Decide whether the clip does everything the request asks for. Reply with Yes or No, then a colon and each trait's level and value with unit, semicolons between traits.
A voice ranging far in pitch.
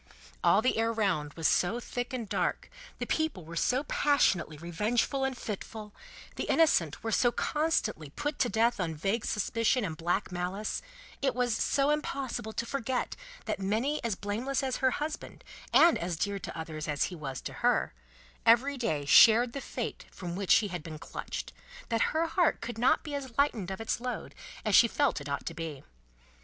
Yes: wide, 6.6 semitones